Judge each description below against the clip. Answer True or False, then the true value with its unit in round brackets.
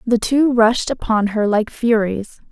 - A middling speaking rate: True (165 wpm)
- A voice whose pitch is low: False (225 Hz)